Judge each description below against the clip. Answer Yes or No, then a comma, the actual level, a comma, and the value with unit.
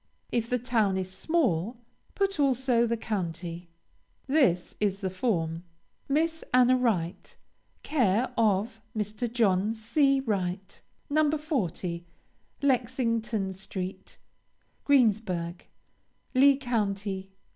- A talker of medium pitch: No, high, 220 Hz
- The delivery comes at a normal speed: No, slow, 100 wpm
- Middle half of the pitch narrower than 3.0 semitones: No, average, 5.2 semitones